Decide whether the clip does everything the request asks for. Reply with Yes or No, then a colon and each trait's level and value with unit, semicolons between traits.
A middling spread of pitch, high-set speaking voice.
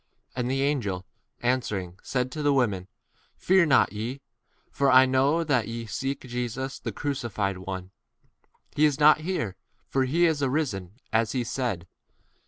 No: average, 4.0 semitones; low, 130 Hz